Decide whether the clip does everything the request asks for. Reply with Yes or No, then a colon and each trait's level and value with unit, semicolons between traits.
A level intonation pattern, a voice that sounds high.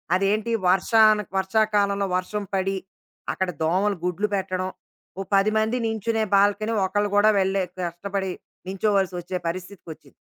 Yes: narrow, 2.1 semitones; high, 195 Hz